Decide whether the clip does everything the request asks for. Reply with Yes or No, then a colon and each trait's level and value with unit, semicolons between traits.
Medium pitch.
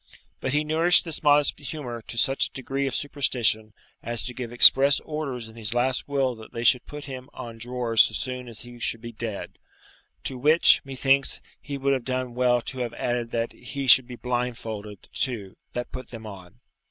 No: low, 125 Hz